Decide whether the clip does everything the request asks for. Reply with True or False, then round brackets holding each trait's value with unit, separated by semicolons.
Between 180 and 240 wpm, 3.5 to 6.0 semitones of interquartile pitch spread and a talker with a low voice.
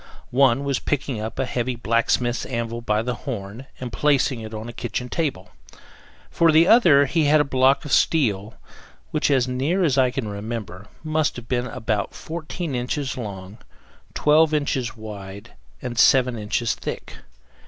False (165 wpm; 4.0 semitones; 125 Hz)